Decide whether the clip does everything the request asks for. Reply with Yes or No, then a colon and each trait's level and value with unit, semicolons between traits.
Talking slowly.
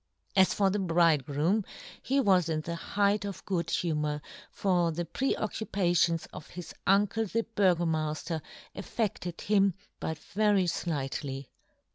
Yes: slow, 130 wpm